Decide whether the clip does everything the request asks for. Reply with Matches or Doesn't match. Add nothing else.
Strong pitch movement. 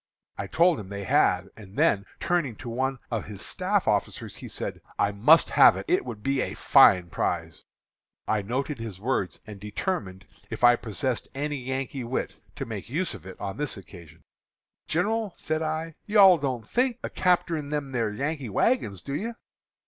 Matches